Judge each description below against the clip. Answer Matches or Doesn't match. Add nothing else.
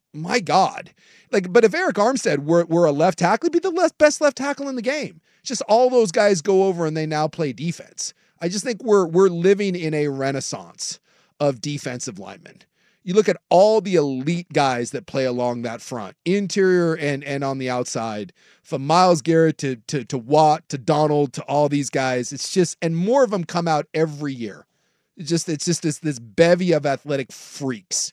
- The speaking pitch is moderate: Matches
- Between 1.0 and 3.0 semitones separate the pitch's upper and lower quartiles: Doesn't match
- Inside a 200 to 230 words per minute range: Matches